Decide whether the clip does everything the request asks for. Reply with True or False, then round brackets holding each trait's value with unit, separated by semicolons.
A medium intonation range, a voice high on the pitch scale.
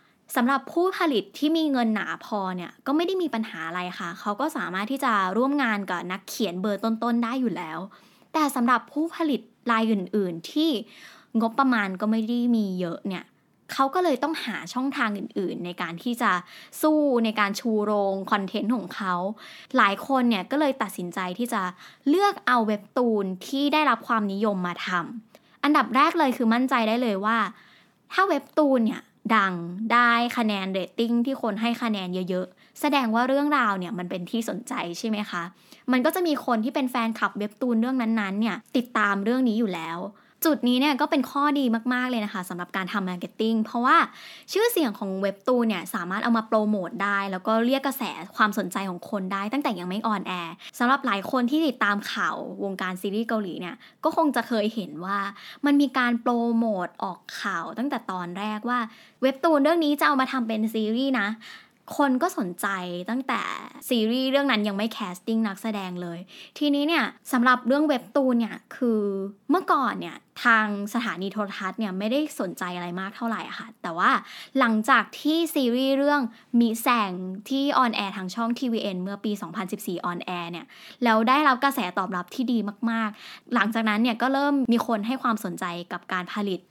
True (4.7 semitones; 225 Hz)